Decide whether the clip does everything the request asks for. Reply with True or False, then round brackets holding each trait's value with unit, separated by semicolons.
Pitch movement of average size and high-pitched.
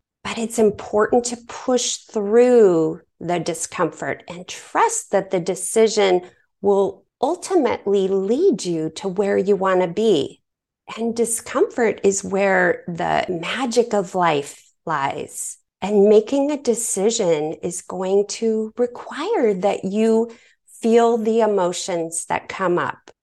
True (4.2 semitones; 205 Hz)